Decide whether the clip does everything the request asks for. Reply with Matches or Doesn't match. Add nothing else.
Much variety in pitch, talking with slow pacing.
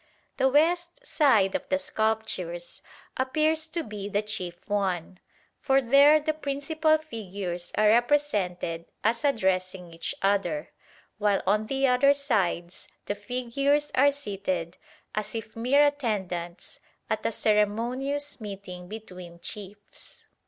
Matches